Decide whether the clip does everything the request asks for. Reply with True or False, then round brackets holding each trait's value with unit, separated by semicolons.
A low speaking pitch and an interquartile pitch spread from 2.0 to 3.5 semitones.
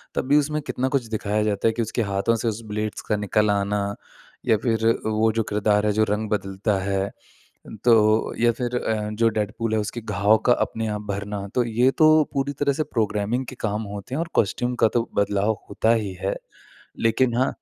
True (110 Hz; 2.6 semitones)